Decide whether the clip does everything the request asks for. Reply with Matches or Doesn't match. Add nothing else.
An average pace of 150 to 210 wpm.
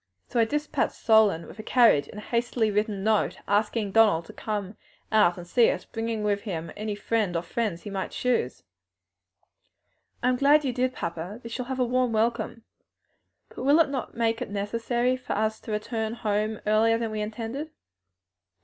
Matches